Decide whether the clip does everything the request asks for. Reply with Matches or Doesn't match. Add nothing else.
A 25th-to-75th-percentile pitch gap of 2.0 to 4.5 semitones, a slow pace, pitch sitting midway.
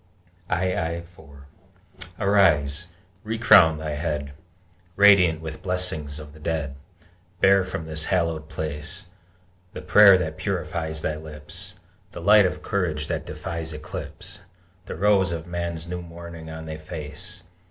Doesn't match